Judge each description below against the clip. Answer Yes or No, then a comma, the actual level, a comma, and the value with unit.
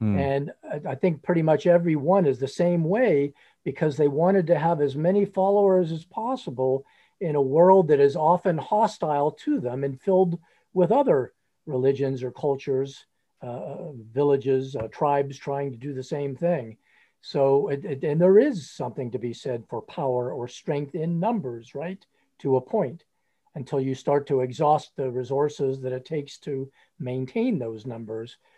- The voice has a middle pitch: Yes, medium, 145 Hz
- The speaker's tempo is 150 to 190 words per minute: Yes, average, 170 wpm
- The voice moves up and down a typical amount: Yes, average, 4.6 semitones